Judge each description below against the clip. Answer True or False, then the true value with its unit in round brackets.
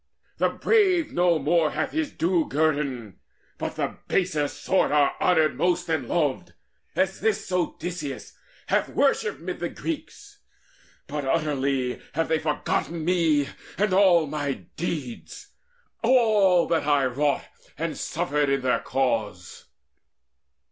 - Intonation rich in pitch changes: False (4.3 semitones)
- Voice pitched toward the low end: False (155 Hz)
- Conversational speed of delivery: False (125 wpm)